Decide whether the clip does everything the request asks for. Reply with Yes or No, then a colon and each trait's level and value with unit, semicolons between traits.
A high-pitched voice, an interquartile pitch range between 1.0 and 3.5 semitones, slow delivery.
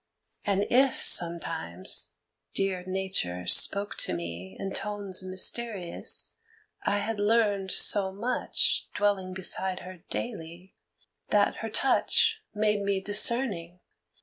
Yes: high, 195 Hz; narrow, 2.5 semitones; slow, 110 wpm